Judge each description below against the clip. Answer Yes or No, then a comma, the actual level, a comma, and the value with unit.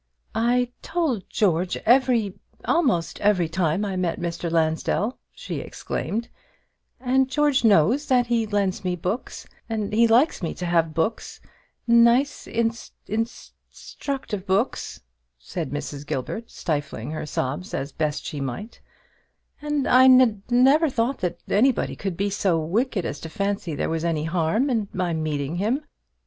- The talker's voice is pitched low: No, high, 205 Hz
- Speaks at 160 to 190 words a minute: No, average, 150 wpm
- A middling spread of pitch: No, wide, 6.6 semitones